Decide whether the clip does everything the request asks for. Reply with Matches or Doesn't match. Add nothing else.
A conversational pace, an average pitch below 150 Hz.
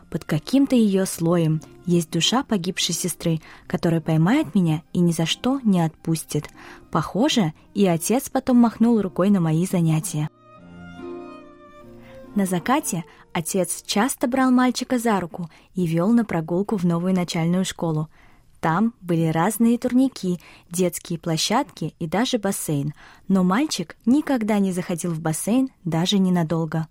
Doesn't match